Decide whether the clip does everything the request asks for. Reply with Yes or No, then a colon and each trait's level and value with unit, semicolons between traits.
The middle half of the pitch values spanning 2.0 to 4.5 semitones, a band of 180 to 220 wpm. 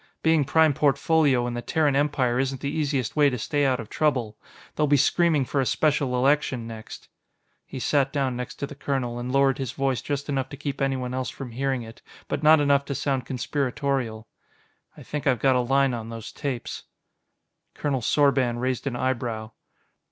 Yes: narrow, 2.4 semitones; average, 190 wpm